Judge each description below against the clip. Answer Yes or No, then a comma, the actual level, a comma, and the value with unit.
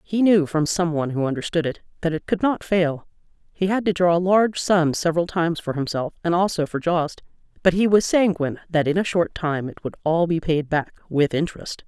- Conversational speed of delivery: No, fast, 220 wpm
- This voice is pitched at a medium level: Yes, medium, 170 Hz